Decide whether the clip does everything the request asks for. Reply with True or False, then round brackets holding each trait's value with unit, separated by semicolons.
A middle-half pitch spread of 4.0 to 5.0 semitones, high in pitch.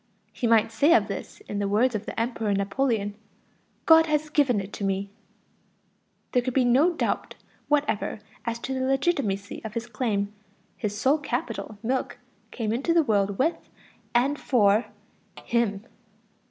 True (4.7 semitones; 235 Hz)